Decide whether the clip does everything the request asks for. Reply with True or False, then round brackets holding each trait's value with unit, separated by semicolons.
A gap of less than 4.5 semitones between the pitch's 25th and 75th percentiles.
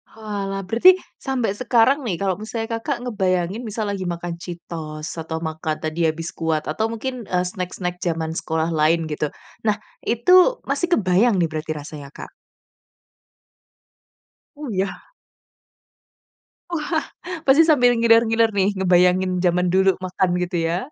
False (5.2 semitones)